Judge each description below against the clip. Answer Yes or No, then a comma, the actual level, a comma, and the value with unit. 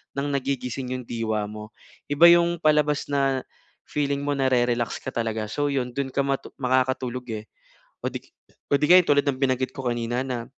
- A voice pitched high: No, low, 130 Hz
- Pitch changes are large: No, narrow, 2.6 semitones